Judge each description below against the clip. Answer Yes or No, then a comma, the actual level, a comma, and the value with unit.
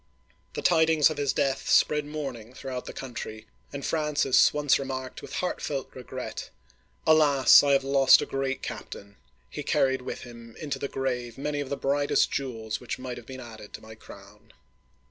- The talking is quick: No, average, 180 wpm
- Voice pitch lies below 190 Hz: Yes, low, 135 Hz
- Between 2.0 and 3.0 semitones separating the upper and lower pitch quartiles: Yes, average, 2.7 semitones